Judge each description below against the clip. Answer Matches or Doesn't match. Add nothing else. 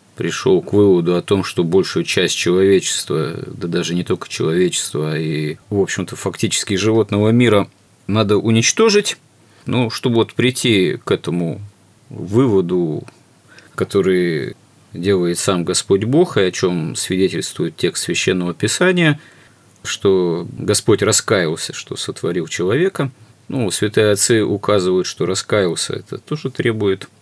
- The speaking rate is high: Doesn't match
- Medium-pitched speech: Doesn't match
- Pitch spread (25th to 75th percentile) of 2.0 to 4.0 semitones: Doesn't match